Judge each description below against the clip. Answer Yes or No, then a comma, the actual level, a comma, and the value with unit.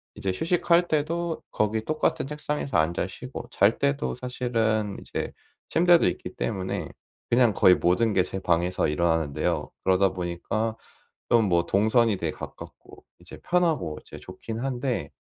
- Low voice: Yes, low, 110 Hz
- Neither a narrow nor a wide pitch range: No, wide, 6.9 semitones